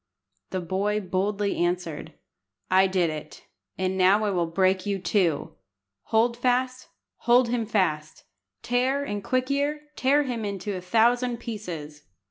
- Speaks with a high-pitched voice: Yes, high, 205 Hz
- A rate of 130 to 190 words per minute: Yes, average, 140 wpm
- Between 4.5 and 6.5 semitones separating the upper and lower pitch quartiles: Yes, average, 4.9 semitones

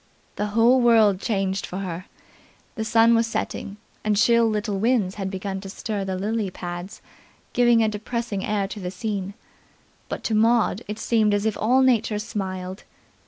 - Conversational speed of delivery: Yes, average, 170 wpm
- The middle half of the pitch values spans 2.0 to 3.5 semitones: Yes, average, 2.8 semitones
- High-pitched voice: Yes, high, 210 Hz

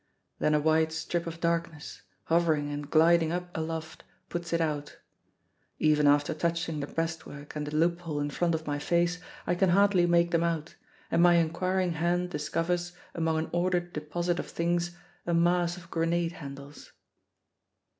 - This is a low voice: No, medium, 165 Hz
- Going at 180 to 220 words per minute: No, average, 165 wpm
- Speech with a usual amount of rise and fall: No, narrow, 1.8 semitones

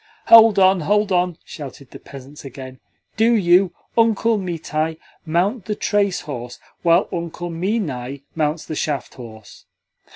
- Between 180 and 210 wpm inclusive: No, slow, 135 wpm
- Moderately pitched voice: Yes, medium, 170 Hz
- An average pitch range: No, wide, 5.8 semitones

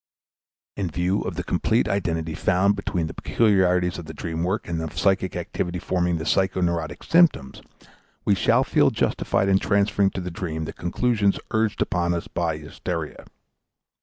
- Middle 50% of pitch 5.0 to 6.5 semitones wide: No, average, 2.8 semitones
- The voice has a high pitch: No, very low, 90 Hz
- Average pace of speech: Yes, average, 165 wpm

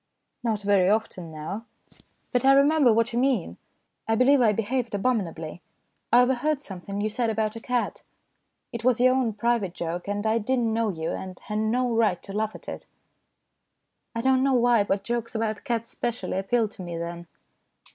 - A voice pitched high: Yes, high, 225 Hz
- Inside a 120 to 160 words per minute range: No, average, 190 wpm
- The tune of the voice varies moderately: Yes, average, 3.5 semitones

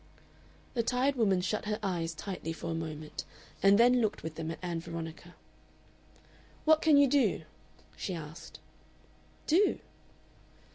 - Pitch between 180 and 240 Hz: Yes, medium, 185 Hz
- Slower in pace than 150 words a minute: Yes, average, 140 wpm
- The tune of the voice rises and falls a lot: Yes, wide, 6.8 semitones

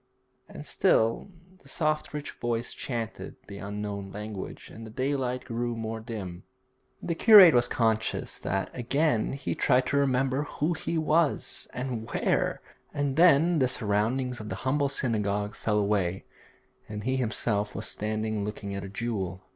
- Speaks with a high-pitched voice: No, low, 115 Hz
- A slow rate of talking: No, average, 155 wpm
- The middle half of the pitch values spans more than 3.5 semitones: Yes, average, 4.5 semitones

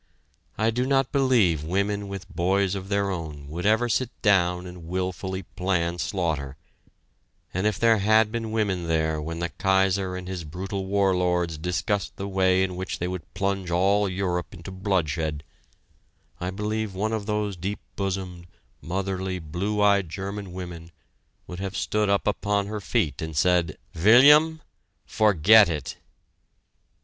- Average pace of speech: Yes, average, 150 wpm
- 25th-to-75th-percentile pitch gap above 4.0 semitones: No, average, 2.7 semitones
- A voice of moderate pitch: No, very low, 95 Hz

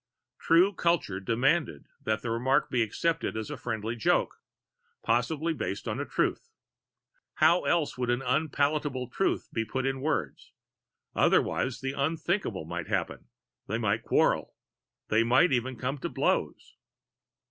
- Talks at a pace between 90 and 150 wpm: Yes, average, 140 wpm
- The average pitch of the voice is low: Yes, low, 130 Hz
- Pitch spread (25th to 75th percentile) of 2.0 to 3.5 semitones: No, wide, 5.4 semitones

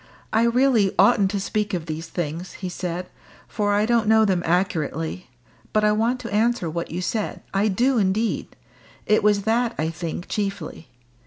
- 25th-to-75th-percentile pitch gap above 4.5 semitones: No, average, 3.8 semitones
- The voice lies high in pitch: Yes, high, 200 Hz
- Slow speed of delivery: No, average, 175 wpm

